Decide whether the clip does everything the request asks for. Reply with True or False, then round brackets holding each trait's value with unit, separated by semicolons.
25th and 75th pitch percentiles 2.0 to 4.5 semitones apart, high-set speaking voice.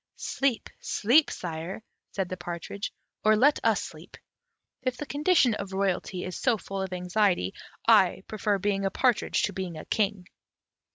True (3.7 semitones; 200 Hz)